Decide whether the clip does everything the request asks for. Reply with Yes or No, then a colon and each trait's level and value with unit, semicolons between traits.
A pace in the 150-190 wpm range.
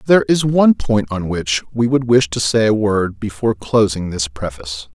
No: fast, 205 wpm